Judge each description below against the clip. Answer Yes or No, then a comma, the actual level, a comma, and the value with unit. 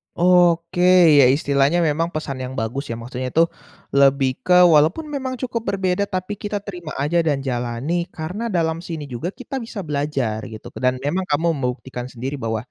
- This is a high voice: No, medium, 155 Hz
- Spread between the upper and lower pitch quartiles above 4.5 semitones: Yes, average, 5.2 semitones